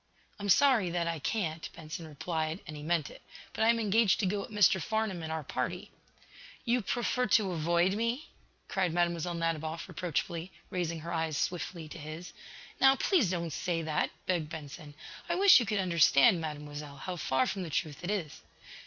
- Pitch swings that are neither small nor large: Yes, average, 3.9 semitones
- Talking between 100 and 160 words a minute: No, average, 185 wpm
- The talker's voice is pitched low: No, medium, 170 Hz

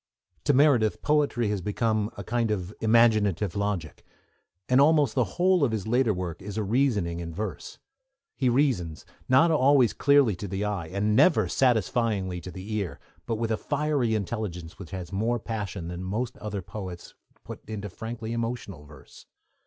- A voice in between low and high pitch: No, low, 110 Hz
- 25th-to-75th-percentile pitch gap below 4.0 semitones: No, average, 4.5 semitones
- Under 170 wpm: No, average, 175 wpm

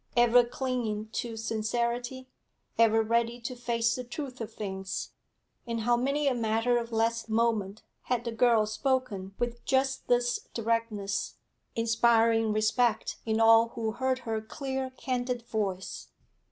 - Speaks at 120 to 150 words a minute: Yes, average, 140 wpm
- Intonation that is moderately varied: No, narrow, 1.8 semitones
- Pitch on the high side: Yes, high, 230 Hz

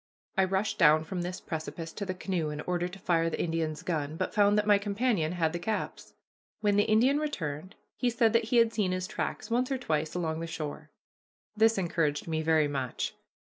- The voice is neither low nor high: Yes, medium, 180 Hz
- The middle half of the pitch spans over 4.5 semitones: Yes, average, 4.9 semitones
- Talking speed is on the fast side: Yes, fast, 210 wpm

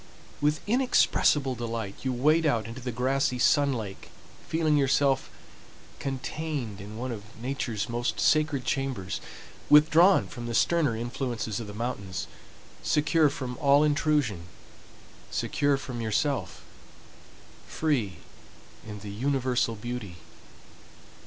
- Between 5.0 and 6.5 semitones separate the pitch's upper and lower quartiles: No, average, 4.2 semitones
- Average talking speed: No, slow, 115 wpm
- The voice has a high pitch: No, low, 130 Hz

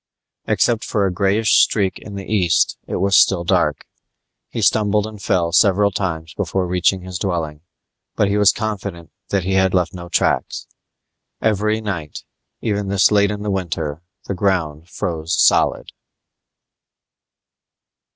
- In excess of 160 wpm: No, average, 145 wpm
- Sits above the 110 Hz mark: No, very low, 95 Hz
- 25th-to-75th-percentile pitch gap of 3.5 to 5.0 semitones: No, average, 2.8 semitones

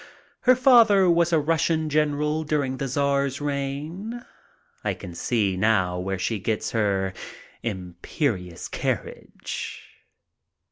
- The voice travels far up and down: Yes, wide, 7.8 semitones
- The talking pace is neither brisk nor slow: No, slow, 110 wpm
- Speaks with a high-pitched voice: No, medium, 140 Hz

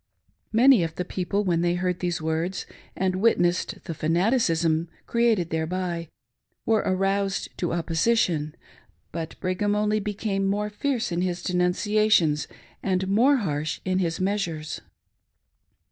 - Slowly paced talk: Yes, slow, 130 wpm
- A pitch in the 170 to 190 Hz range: Yes, medium, 185 Hz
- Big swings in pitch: No, average, 3.6 semitones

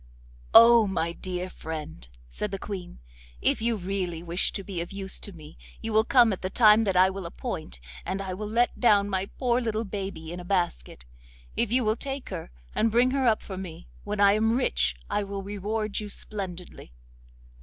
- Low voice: No, high, 200 Hz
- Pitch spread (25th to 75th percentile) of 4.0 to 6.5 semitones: No, average, 3.5 semitones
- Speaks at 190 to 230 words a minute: Yes, average, 200 wpm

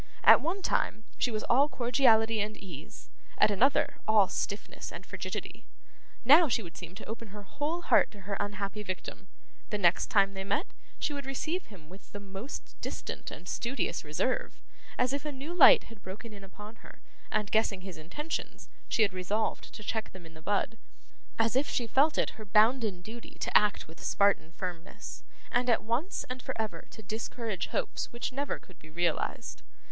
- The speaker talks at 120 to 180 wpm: No, average, 190 wpm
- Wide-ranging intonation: No, average, 4.4 semitones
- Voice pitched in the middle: No, high, 215 Hz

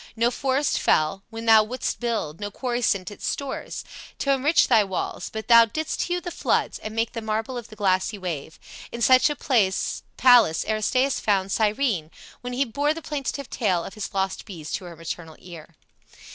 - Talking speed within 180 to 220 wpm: Yes, average, 185 wpm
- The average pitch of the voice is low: No, high, 220 Hz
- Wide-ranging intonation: No, average, 5.0 semitones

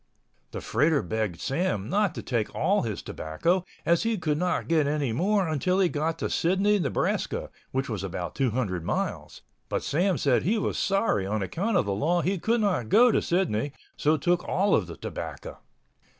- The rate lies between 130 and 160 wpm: No, average, 190 wpm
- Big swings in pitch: Yes, wide, 8.5 semitones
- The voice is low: No, medium, 160 Hz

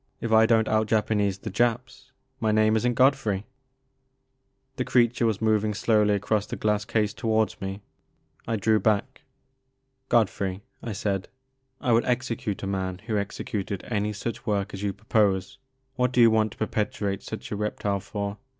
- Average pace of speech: Yes, average, 170 wpm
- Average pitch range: No, narrow, 2.1 semitones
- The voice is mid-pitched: No, low, 110 Hz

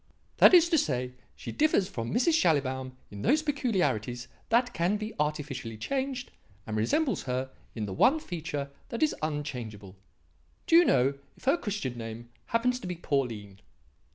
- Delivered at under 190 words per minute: Yes, average, 165 wpm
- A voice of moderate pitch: Yes, medium, 150 Hz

